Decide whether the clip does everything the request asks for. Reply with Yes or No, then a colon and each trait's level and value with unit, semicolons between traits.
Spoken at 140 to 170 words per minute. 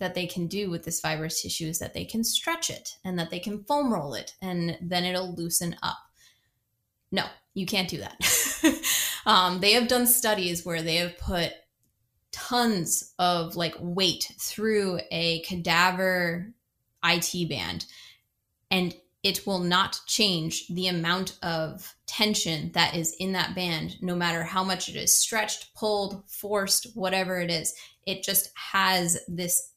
Yes: average, 160 wpm